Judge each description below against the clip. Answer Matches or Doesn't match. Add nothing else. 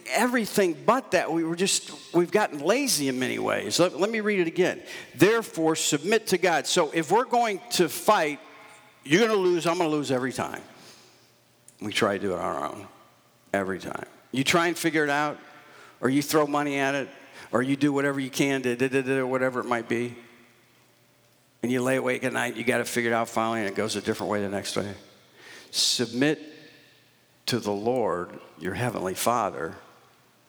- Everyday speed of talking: Matches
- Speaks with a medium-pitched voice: Matches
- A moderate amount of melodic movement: Doesn't match